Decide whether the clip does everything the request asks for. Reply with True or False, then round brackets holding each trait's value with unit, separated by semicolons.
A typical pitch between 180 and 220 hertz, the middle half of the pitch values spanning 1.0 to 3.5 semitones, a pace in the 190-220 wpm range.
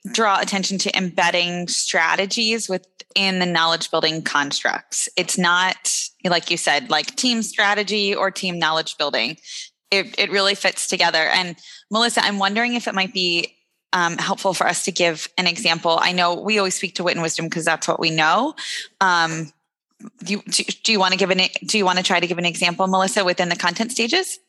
True (185 Hz; 2.8 semitones; 200 wpm)